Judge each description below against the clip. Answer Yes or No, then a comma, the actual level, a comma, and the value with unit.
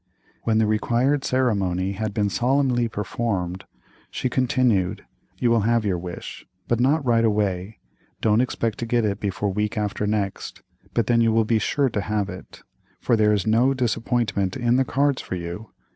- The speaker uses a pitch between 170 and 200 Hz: No, low, 110 Hz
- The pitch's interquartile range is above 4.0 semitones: No, average, 3.2 semitones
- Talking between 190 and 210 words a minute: No, average, 175 wpm